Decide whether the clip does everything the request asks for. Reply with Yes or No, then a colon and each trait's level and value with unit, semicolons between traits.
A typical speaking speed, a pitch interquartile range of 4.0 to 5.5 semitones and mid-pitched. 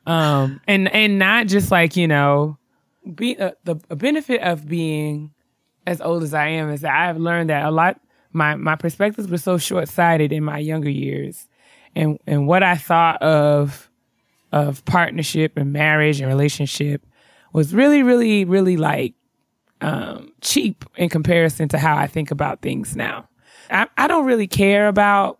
Yes: average, 170 wpm; average, 4.3 semitones; medium, 165 Hz